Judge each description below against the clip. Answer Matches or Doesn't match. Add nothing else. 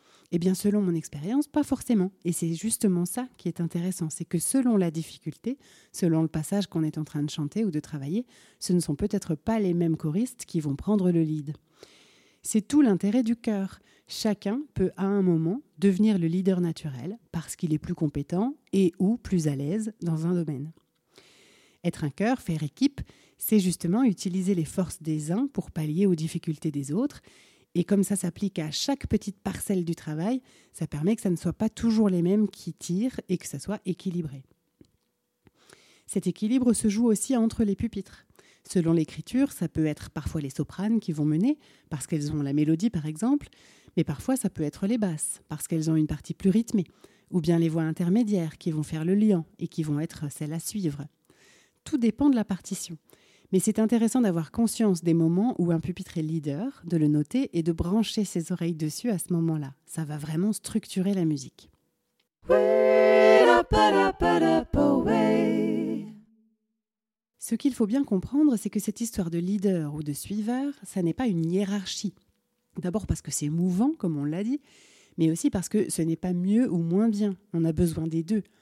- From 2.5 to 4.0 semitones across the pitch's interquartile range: Doesn't match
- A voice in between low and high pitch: Matches